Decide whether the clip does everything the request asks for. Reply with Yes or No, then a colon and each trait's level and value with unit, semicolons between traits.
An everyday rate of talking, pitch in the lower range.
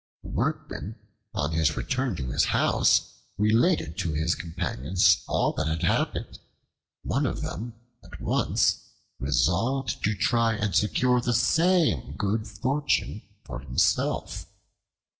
No: slow, 125 wpm; low, 100 Hz